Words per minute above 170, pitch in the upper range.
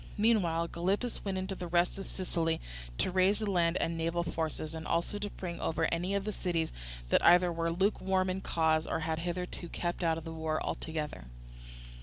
No: average, 195 wpm; medium, 175 Hz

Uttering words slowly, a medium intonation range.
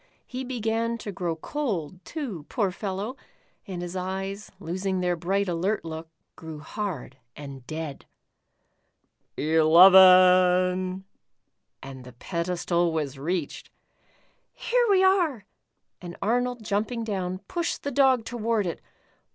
Yes: slow, 120 wpm; average, 4.9 semitones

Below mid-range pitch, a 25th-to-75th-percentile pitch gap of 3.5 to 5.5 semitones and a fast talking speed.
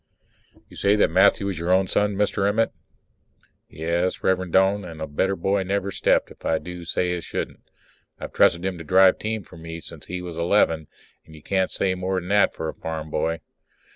No: very low, 90 Hz; average, 2.8 semitones; fast, 210 wpm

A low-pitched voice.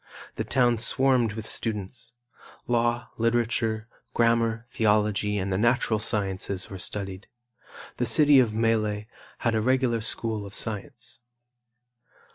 Yes: low, 115 Hz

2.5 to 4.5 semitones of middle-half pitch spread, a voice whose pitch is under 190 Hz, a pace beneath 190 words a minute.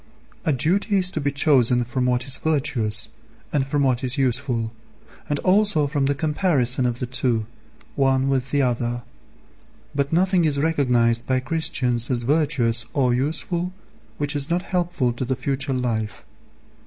Yes: average, 3.8 semitones; low, 135 Hz; average, 160 wpm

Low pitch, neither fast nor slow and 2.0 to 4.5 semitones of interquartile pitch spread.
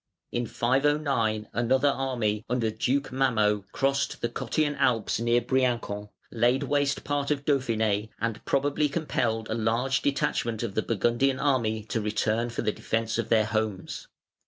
Yes: low, 120 Hz; average, 150 wpm; average, 3.7 semitones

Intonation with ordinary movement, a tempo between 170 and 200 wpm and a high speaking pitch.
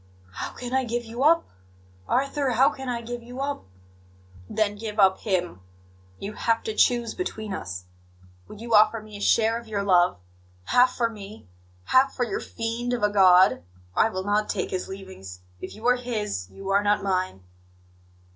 Yes: average, 3.6 semitones; average, 185 wpm; high, 215 Hz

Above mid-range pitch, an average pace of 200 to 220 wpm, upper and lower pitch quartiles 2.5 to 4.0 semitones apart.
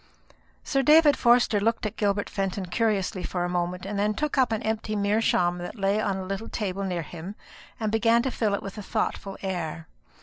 Yes: high, 205 Hz; fast, 205 wpm; average, 3.1 semitones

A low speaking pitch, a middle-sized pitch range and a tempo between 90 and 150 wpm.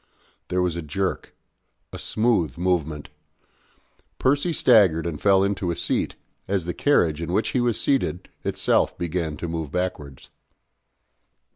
Yes: very low, 90 Hz; average, 3.6 semitones; average, 140 wpm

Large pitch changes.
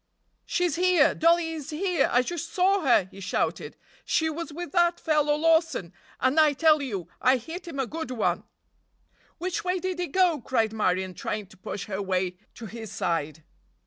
Yes: wide, 8.0 semitones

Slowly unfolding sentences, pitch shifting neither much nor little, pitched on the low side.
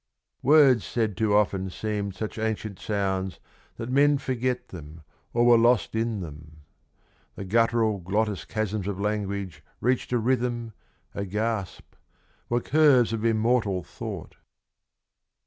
Yes: slow, 130 wpm; average, 3.3 semitones; low, 110 Hz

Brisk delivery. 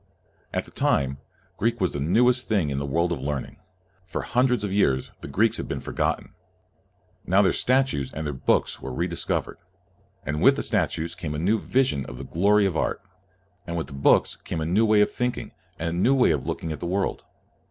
Yes: fast, 220 wpm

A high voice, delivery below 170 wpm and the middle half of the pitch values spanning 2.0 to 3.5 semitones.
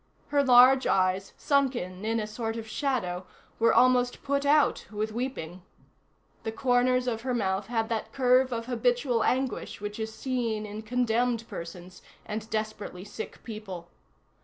Yes: high, 230 Hz; average, 150 wpm; average, 3.0 semitones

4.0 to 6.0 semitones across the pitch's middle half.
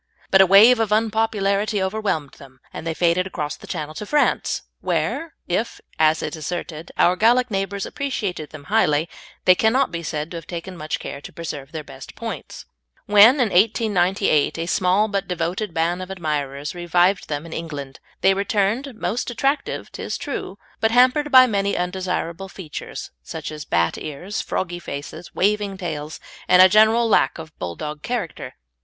Yes: average, 5.2 semitones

